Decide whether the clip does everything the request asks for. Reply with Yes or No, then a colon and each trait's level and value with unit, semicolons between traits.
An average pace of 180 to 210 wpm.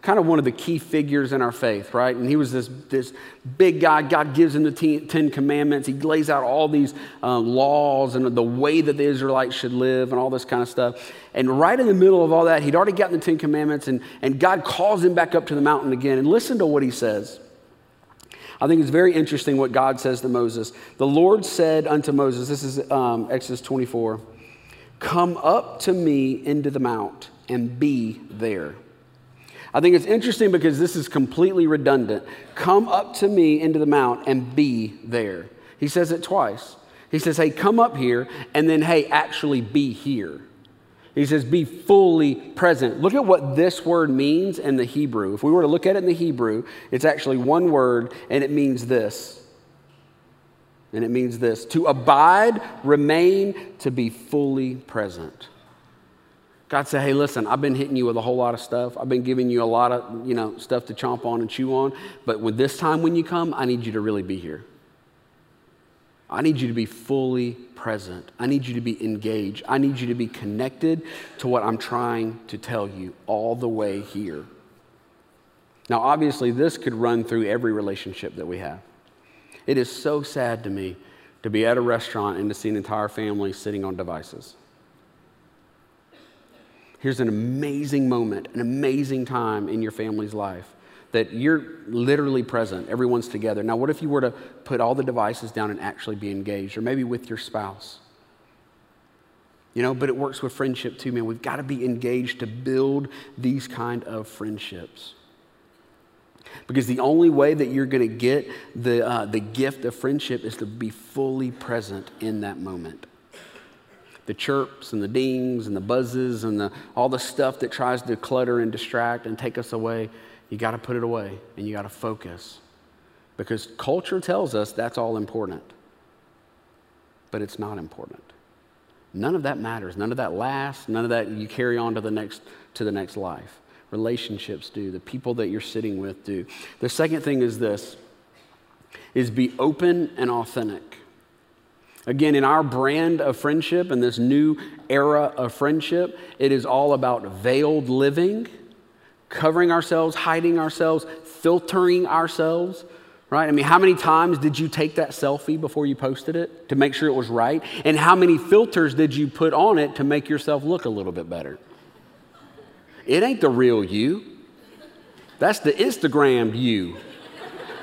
Yes: average, 190 wpm